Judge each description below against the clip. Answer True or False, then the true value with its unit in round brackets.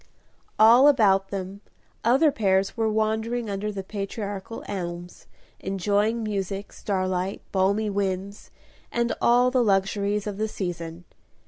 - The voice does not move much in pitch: True (2.3 semitones)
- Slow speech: True (120 wpm)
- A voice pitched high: True (200 Hz)